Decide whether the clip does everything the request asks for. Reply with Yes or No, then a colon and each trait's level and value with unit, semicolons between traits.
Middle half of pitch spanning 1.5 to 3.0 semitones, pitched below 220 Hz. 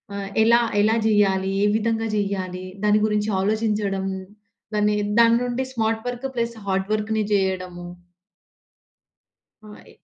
Yes: narrow, 2.4 semitones; high, 210 Hz